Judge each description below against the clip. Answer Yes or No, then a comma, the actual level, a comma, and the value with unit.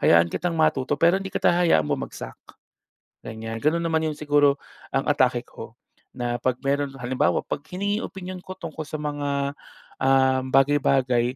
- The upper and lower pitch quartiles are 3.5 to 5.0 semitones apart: Yes, average, 4.1 semitones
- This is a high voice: No, medium, 145 Hz